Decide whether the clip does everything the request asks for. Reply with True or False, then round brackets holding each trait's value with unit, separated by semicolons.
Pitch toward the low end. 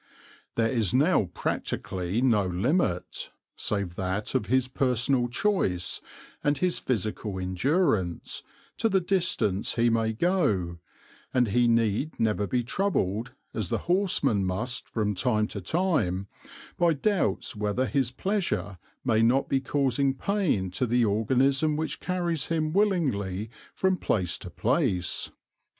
True (120 Hz)